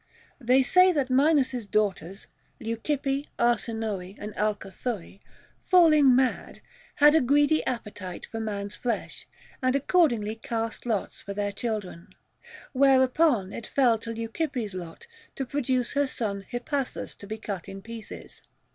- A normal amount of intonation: Yes, average, 4.6 semitones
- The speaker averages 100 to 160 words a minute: Yes, average, 140 wpm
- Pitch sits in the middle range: No, high, 235 Hz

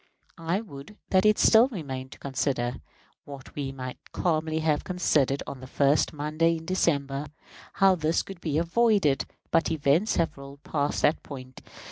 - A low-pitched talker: No, medium, 150 Hz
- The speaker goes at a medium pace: Yes, average, 160 wpm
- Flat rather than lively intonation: No, average, 3.7 semitones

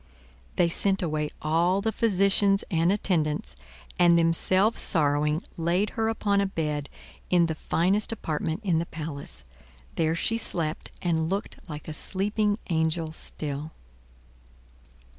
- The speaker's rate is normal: No, slow, 130 wpm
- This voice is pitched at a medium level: Yes, medium, 170 Hz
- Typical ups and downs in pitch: Yes, average, 4.0 semitones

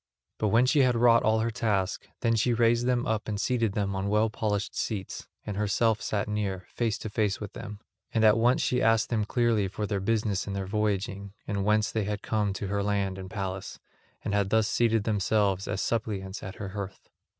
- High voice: No, low, 105 Hz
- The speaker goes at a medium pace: No, fast, 215 wpm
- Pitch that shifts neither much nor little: No, narrow, 2.3 semitones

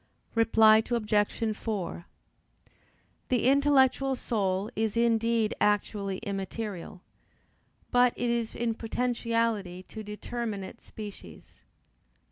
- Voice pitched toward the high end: Yes, high, 220 Hz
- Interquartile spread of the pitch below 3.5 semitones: Yes, narrow, 2.4 semitones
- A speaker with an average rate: No, slow, 90 wpm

